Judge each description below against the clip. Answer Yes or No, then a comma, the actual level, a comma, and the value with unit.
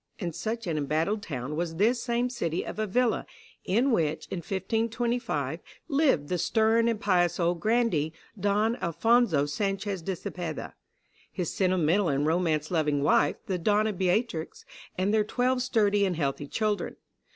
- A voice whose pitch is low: No, high, 190 Hz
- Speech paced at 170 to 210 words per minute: No, average, 150 wpm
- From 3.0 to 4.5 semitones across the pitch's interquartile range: No, wide, 5.5 semitones